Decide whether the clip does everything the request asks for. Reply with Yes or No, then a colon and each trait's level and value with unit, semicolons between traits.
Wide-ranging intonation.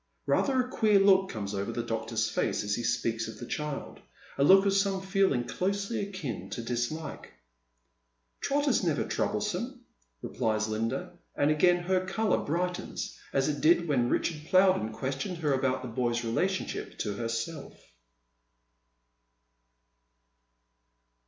Yes: wide, 8.6 semitones